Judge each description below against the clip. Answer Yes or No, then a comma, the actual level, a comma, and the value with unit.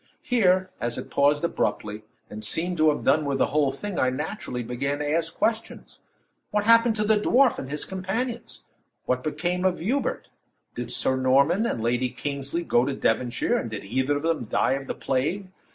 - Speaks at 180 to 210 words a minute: Yes, average, 185 wpm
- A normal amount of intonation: No, wide, 6.4 semitones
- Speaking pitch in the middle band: Yes, medium, 150 Hz